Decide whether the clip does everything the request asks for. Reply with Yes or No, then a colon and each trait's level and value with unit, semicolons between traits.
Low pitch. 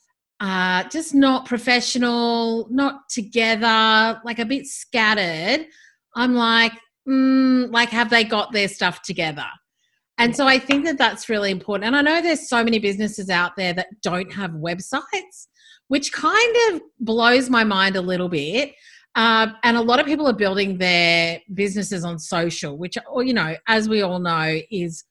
No: high, 230 Hz